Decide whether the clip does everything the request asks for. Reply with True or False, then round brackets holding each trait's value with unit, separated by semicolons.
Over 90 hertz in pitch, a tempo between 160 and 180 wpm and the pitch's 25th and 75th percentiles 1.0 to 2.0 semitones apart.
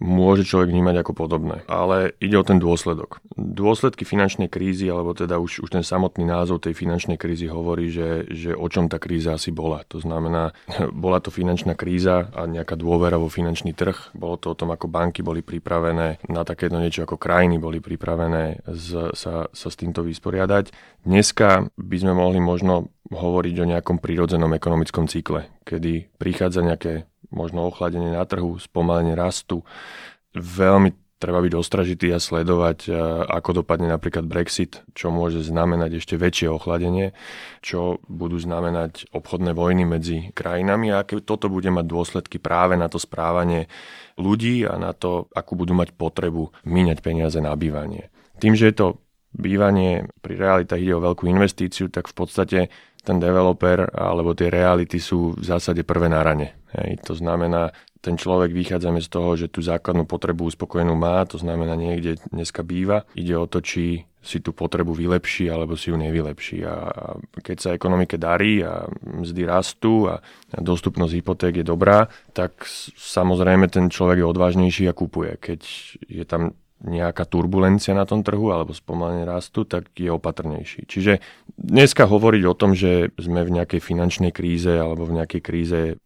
False (85 Hz; 165 wpm; 1.4 semitones)